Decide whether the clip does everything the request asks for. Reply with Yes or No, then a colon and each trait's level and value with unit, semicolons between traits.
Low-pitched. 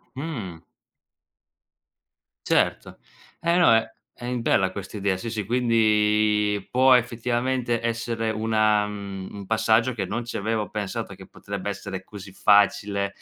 Yes: low, 110 Hz